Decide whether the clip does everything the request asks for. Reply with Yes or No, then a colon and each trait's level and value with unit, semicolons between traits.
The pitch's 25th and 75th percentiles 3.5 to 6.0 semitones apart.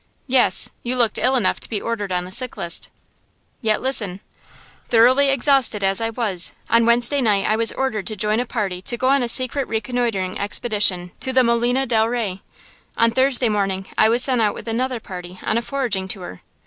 Yes: average, 3.8 semitones